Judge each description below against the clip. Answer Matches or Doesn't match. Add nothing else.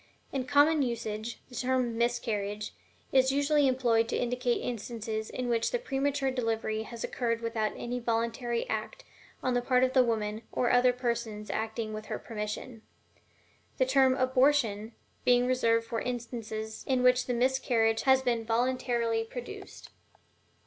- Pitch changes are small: Matches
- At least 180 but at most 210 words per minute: Doesn't match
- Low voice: Doesn't match